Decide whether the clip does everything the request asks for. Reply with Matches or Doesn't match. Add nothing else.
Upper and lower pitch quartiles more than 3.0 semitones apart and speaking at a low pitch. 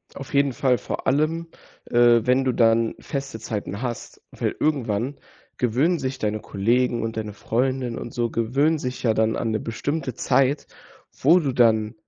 Matches